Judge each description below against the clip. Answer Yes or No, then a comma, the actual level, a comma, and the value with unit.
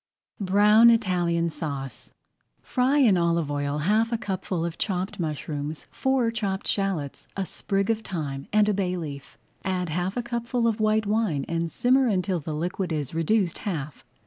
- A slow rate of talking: No, average, 165 wpm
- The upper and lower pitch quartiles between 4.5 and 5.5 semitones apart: Yes, average, 5.0 semitones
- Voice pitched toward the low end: No, medium, 185 Hz